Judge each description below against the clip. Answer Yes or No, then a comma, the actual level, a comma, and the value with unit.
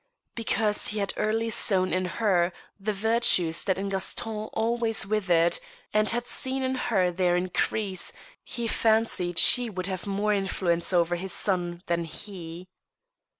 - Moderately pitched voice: No, high, 195 Hz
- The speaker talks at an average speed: Yes, average, 150 wpm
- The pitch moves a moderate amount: Yes, average, 3.6 semitones